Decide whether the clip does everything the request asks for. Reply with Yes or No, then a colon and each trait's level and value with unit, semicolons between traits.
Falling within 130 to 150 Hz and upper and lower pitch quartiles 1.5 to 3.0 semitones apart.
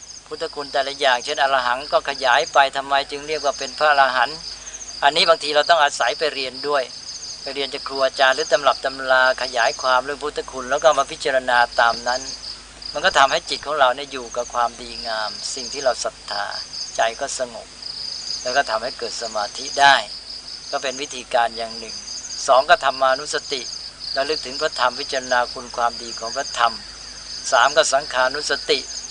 Yes: low, 135 Hz; average, 2.7 semitones